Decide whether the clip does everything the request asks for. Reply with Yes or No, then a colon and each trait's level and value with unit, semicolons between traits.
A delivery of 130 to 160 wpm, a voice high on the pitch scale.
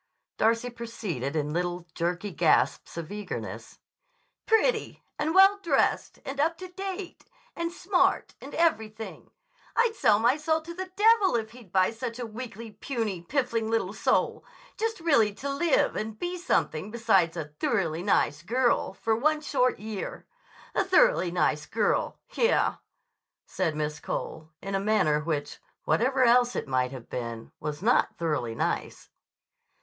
Yes: average, 150 wpm; high, 225 Hz